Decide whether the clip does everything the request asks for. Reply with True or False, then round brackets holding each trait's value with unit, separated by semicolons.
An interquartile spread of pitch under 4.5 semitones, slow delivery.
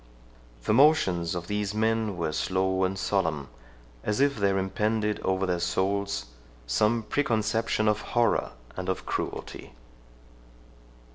True (2.8 semitones; 125 wpm)